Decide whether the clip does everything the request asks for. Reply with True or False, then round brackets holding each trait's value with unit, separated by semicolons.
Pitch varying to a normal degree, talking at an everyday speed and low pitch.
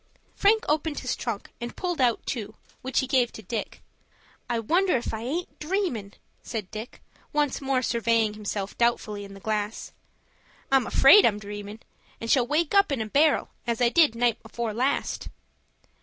False (4.9 semitones; 170 wpm; 240 Hz)